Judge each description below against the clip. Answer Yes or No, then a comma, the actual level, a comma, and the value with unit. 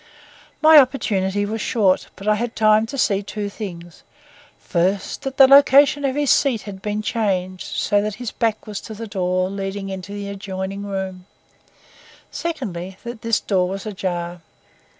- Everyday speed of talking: Yes, average, 165 wpm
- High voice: Yes, high, 205 Hz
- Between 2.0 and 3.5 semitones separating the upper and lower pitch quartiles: Yes, average, 3.2 semitones